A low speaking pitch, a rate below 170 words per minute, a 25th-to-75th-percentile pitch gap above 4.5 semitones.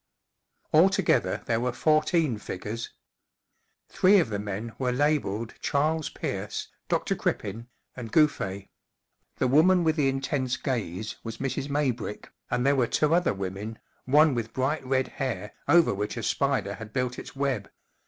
Yes: low, 130 Hz; average, 150 wpm; average, 5.2 semitones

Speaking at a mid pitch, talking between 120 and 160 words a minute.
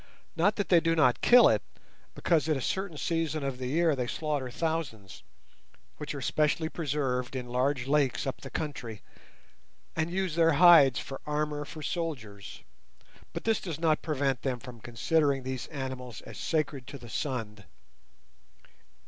Yes: medium, 145 Hz; average, 155 wpm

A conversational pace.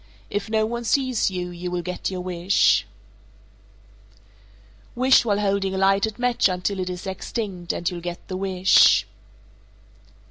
Yes: average, 150 wpm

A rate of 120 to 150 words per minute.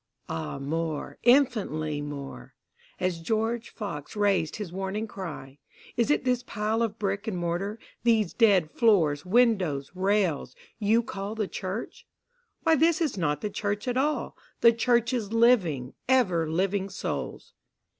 Yes: average, 145 wpm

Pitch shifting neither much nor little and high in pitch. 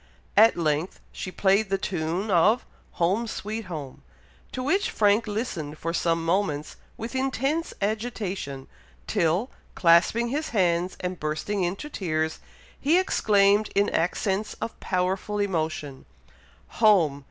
Yes: average, 4.7 semitones; high, 195 Hz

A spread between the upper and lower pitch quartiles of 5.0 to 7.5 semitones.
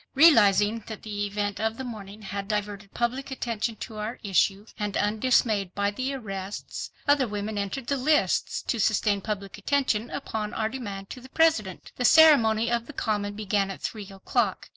No: average, 3.0 semitones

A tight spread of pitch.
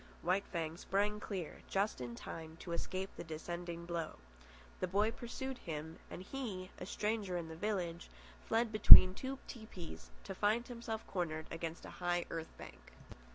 No: average, 4.1 semitones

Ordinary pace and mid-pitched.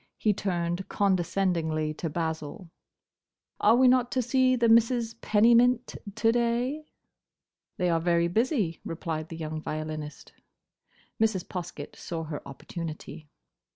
No: slow, 120 wpm; medium, 180 Hz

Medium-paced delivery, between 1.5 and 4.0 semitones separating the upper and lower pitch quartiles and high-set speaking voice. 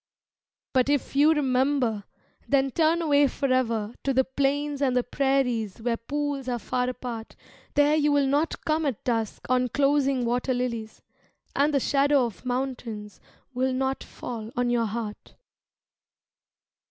Yes: average, 145 wpm; average, 2.9 semitones; very high, 260 Hz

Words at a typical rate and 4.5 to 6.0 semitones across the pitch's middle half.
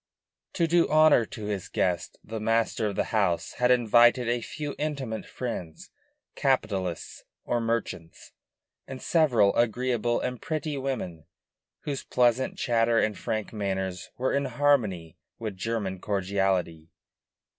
No: slow, 130 wpm; average, 4.8 semitones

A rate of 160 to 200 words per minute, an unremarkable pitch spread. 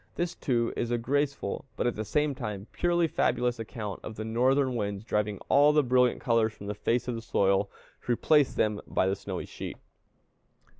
Yes: average, 195 wpm; average, 4.2 semitones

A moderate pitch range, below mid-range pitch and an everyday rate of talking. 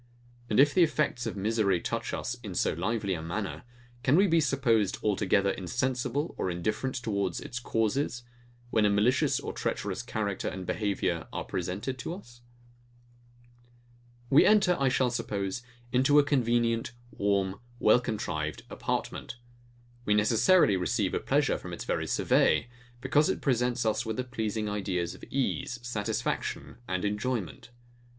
Yes: average, 4.2 semitones; low, 110 Hz; average, 150 wpm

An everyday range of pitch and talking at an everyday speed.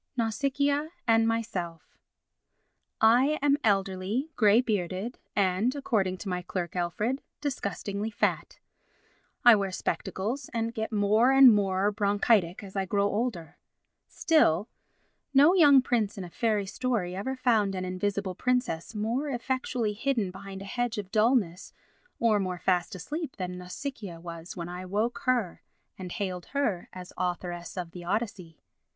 Yes: average, 4.7 semitones; average, 145 wpm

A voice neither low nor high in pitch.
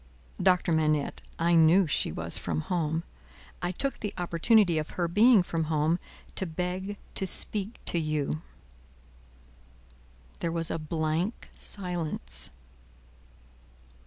Yes: medium, 170 Hz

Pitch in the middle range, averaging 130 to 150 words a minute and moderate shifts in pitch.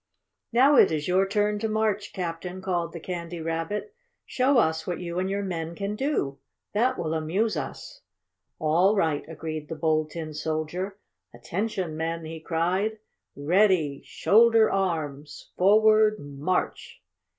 Yes: medium, 180 Hz; average, 140 wpm; average, 4.6 semitones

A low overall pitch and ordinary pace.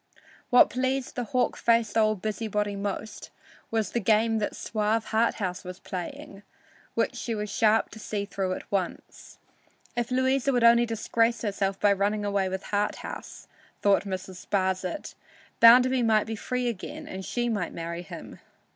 No: high, 215 Hz; average, 160 wpm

